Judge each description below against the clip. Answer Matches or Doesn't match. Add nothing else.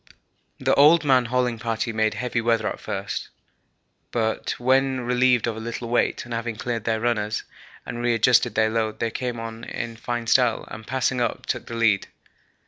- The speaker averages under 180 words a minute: Doesn't match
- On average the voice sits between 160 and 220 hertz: Doesn't match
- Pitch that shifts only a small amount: Matches